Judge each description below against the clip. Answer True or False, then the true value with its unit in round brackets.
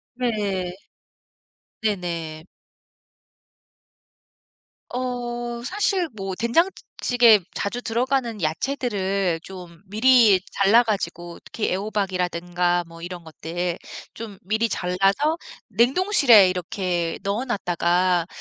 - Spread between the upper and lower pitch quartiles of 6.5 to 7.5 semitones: False (5.2 semitones)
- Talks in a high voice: True (200 Hz)